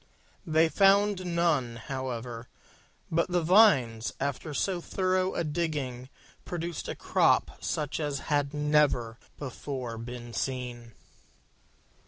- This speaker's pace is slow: Yes, slow, 110 wpm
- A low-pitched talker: No, medium, 145 Hz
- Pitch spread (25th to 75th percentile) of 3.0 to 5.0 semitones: No, wide, 5.6 semitones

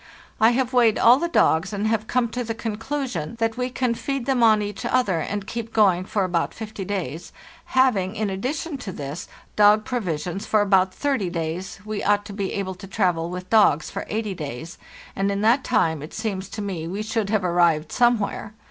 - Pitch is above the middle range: Yes, high, 205 Hz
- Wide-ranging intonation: No, average, 4.0 semitones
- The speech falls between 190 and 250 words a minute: Yes, average, 200 wpm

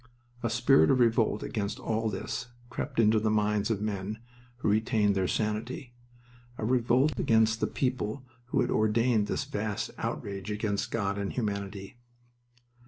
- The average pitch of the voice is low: Yes, low, 110 Hz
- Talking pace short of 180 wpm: Yes, average, 150 wpm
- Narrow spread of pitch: Yes, narrow, 2.2 semitones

